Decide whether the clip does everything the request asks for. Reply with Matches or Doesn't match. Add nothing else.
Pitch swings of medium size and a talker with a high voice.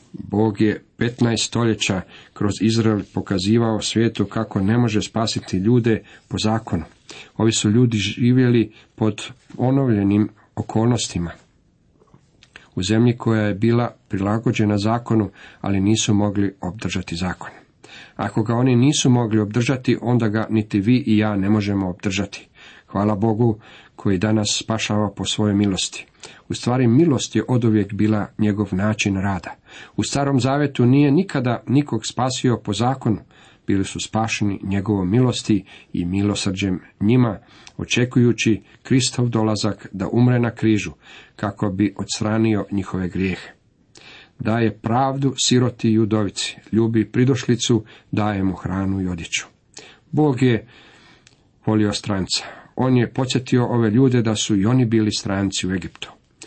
Doesn't match